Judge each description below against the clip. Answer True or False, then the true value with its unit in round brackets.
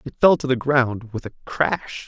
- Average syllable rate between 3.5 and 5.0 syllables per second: True (4.3 syllables/s)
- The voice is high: False (130 Hz)